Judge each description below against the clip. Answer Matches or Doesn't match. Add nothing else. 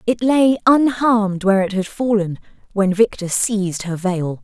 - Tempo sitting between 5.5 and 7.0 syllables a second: Doesn't match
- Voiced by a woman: Matches